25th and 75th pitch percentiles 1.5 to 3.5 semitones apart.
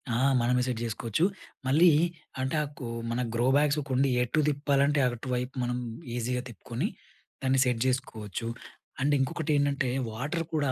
Yes: average, 2.7 semitones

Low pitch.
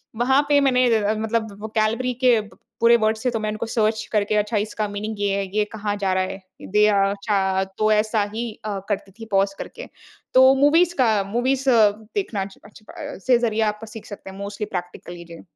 No: high, 215 Hz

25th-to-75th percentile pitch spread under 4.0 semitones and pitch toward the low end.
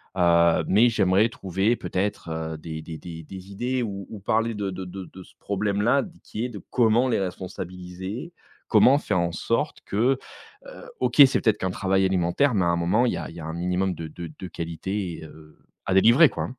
No: average, 4.5 semitones; very low, 95 Hz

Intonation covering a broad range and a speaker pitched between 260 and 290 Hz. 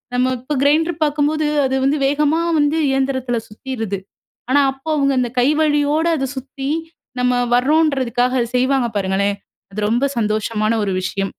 No: average, 3.7 semitones; very high, 265 Hz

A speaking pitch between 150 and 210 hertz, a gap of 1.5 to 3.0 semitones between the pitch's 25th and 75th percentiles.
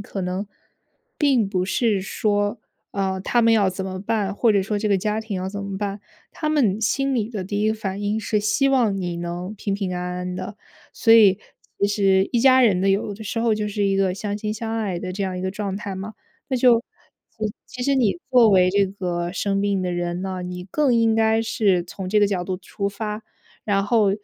Yes: high, 205 Hz; narrow, 2.6 semitones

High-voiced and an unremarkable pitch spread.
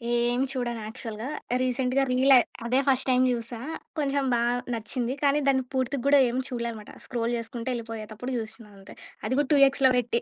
No: high, 245 Hz; narrow, 2.2 semitones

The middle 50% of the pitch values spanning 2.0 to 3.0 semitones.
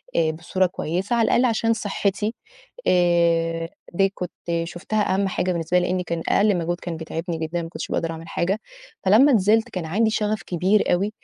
No: average, 3.7 semitones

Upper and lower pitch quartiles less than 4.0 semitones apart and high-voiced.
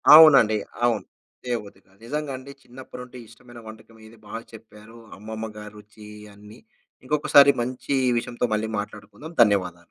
No: average, 3.1 semitones; low, 115 Hz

